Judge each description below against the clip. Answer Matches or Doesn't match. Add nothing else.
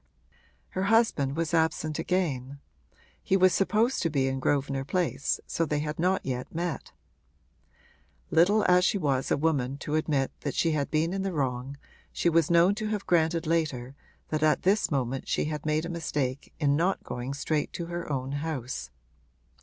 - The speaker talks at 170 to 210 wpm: Matches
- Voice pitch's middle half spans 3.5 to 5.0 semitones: Matches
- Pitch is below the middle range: Doesn't match